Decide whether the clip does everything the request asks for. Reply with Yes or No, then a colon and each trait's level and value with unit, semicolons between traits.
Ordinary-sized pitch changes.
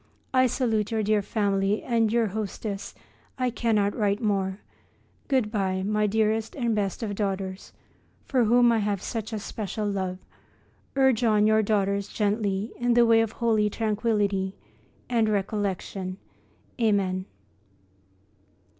No: narrow, 2.1 semitones